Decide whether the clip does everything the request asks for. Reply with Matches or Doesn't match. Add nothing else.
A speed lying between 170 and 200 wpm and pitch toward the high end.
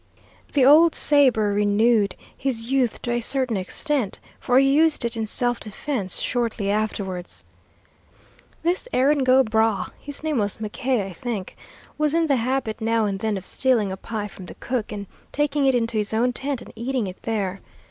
Matches